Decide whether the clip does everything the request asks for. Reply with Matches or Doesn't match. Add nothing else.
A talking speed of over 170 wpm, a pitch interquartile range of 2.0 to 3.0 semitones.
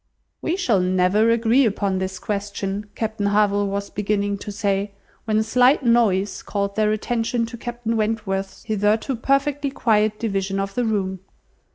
Doesn't match